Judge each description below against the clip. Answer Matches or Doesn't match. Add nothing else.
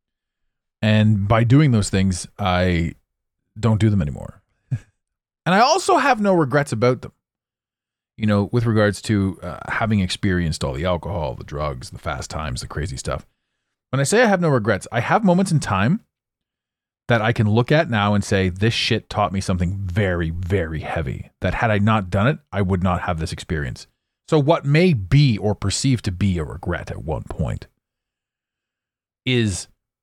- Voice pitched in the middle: Doesn't match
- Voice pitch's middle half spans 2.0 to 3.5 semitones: Doesn't match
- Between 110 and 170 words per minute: Doesn't match